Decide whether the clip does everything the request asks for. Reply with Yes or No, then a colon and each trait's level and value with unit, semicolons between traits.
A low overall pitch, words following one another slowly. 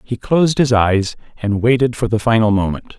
No: low, 115 Hz; average, 200 wpm